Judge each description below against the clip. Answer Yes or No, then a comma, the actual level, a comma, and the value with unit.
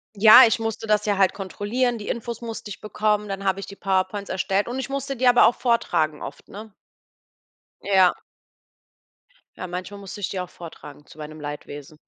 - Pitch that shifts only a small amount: No, average, 3.3 semitones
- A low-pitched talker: No, high, 200 Hz